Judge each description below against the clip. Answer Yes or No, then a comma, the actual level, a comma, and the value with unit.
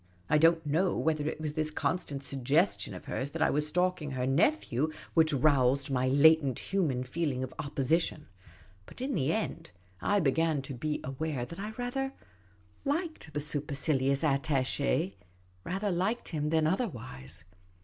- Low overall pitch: No, medium, 150 Hz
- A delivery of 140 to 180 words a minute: Yes, average, 150 wpm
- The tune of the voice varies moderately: Yes, average, 3.9 semitones